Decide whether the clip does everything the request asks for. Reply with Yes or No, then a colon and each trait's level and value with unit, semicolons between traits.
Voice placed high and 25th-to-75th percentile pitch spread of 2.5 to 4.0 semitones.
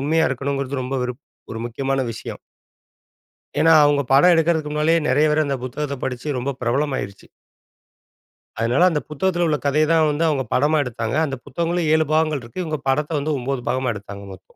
No: medium, 140 Hz; average, 3.3 semitones